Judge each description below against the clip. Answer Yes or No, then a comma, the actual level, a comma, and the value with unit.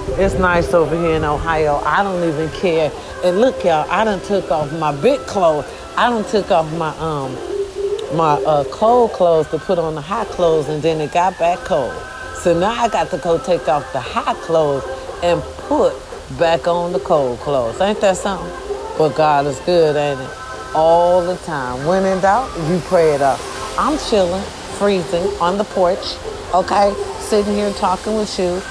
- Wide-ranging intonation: No, average, 3.8 semitones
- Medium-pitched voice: Yes, medium, 175 Hz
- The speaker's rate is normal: Yes, average, 190 wpm